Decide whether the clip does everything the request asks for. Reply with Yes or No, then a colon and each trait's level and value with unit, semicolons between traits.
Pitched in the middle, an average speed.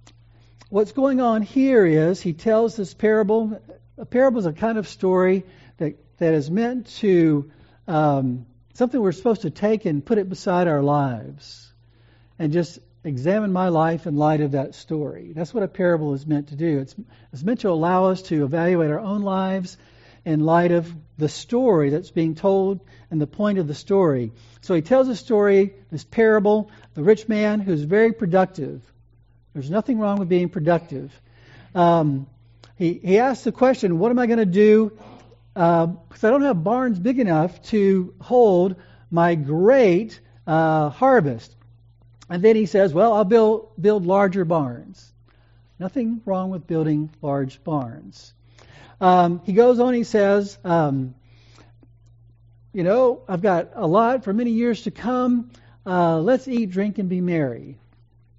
Yes: medium, 170 Hz; average, 165 wpm